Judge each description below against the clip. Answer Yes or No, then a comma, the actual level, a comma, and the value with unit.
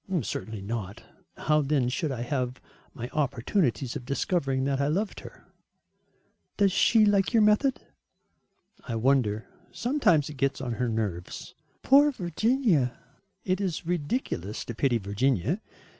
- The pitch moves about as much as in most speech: No, wide, 7.8 semitones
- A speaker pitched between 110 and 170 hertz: Yes, medium, 140 Hz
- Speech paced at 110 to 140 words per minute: Yes, slow, 135 wpm